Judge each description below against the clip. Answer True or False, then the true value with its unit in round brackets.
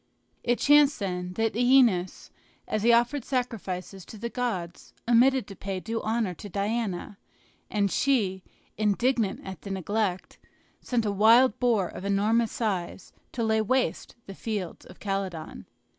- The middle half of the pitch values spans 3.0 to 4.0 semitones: True (3.6 semitones)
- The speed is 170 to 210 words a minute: False (145 wpm)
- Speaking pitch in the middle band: False (215 Hz)